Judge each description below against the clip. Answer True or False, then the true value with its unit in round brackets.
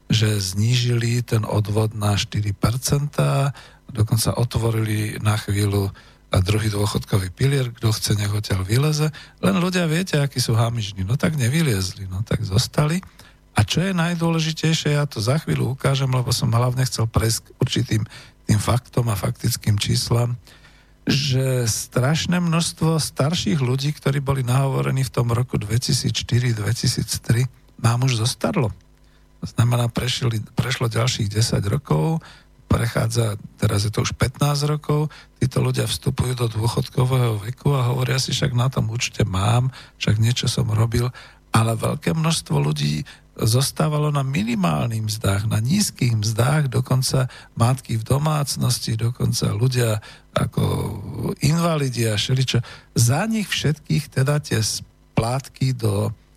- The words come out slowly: False (135 wpm)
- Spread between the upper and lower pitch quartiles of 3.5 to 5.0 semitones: True (3.8 semitones)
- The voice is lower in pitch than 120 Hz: False (125 Hz)